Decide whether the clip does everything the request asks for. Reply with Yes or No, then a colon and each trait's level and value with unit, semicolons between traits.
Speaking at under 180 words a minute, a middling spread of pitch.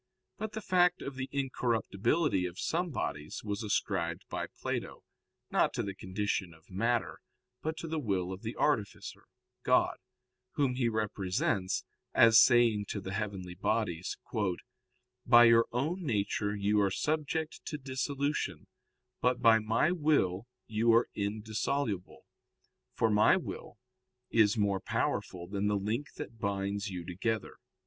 Yes: average, 140 wpm; average, 4.9 semitones